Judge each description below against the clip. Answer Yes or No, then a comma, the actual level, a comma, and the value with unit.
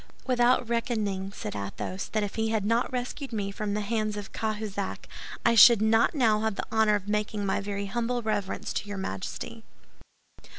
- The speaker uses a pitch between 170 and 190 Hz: No, high, 215 Hz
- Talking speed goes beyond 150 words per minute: Yes, average, 180 wpm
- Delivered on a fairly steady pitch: Yes, narrow, 2.3 semitones